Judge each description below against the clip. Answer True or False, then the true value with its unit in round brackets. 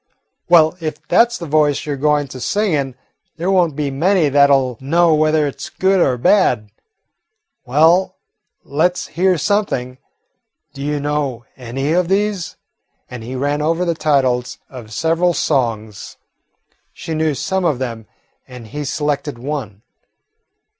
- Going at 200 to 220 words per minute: False (155 wpm)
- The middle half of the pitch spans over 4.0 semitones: True (4.4 semitones)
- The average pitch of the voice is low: False (150 Hz)